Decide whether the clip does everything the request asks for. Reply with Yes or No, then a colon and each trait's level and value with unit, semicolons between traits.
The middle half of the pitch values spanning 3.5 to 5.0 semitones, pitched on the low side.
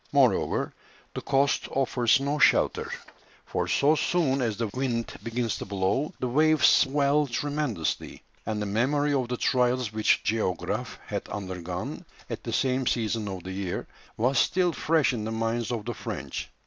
Yes: average, 4.4 semitones; low, 120 Hz